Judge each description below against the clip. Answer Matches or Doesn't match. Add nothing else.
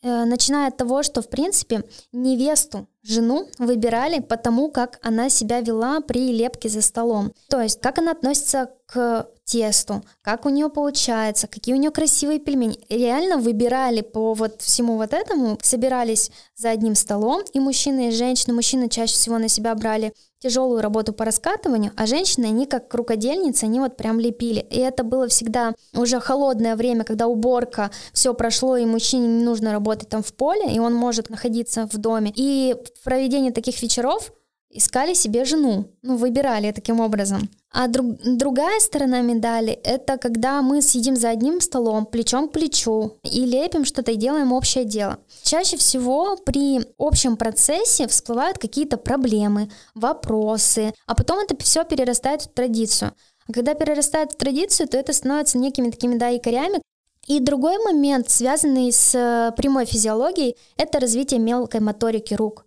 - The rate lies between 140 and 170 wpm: Matches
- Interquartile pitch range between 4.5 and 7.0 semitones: Doesn't match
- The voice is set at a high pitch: Matches